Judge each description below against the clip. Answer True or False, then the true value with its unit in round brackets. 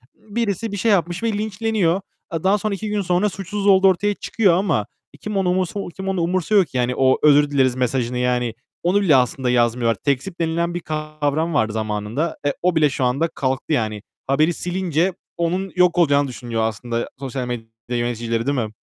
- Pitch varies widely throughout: True (7.2 semitones)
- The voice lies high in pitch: False (160 Hz)